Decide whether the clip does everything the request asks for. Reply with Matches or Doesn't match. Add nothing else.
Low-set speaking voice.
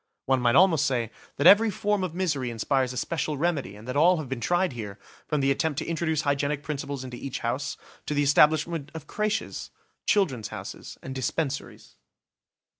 Doesn't match